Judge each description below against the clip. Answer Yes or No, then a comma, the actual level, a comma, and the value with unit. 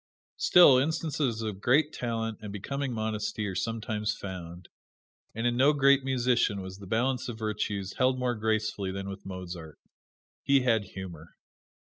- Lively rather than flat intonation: No, average, 4.5 semitones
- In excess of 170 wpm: No, average, 150 wpm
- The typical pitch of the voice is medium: No, low, 110 Hz